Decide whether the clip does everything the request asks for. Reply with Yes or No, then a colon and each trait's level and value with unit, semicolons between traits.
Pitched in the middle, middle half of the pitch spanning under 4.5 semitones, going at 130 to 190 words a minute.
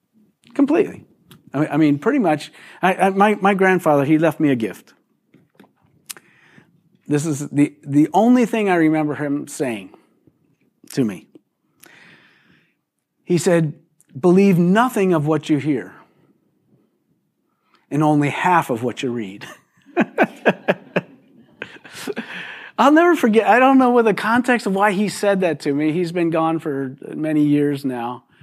No: medium, 160 Hz; wide, 5.5 semitones; slow, 135 wpm